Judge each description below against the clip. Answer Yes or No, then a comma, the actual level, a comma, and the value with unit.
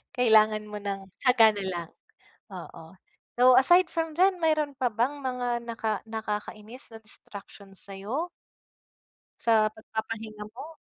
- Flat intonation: No, average, 3.3 semitones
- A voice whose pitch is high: Yes, high, 225 Hz